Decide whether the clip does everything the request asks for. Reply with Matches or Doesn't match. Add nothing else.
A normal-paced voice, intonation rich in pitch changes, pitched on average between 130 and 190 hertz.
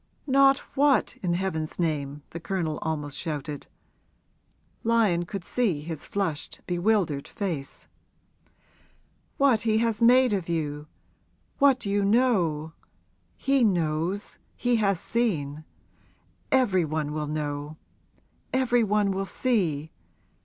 Doesn't match